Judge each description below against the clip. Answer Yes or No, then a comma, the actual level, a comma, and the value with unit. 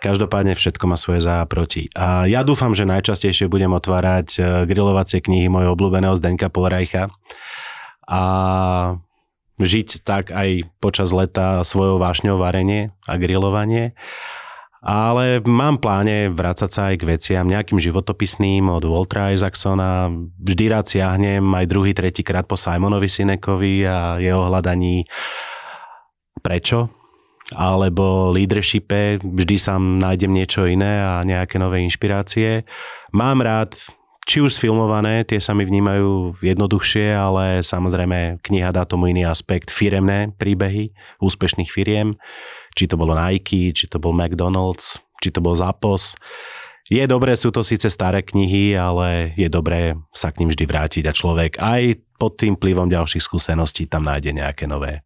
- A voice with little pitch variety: Yes, narrow, 2.1 semitones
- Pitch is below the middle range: Yes, very low, 95 Hz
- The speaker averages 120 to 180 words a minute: Yes, average, 140 wpm